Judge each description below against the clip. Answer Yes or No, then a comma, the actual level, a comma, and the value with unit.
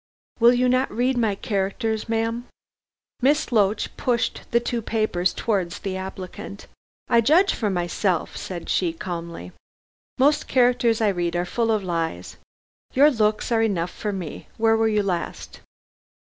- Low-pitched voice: No, high, 215 Hz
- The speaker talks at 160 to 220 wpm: No, average, 150 wpm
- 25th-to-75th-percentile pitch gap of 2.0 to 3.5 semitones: No, average, 4.3 semitones